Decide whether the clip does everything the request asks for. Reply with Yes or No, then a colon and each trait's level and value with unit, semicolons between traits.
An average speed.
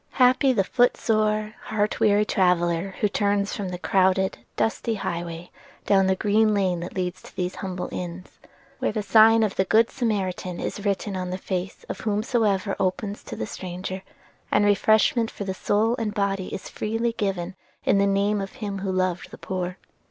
Yes: average, 180 wpm